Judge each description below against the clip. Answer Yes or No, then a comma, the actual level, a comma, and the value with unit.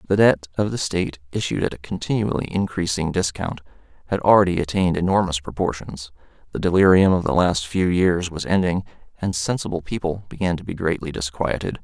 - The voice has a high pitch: No, very low, 90 Hz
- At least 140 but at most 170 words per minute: Yes, average, 165 wpm